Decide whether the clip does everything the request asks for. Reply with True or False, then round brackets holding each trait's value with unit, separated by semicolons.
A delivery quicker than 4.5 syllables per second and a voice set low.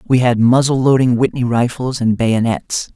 True (4.7 syllables/s; 125 Hz)